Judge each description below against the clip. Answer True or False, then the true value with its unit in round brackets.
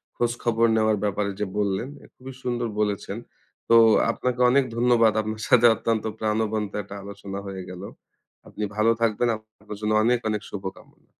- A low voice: True (110 Hz)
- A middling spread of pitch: False (2.3 semitones)